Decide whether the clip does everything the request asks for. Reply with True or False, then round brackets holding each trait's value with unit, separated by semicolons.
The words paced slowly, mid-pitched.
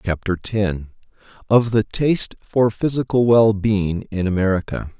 False (120 wpm; 105 Hz)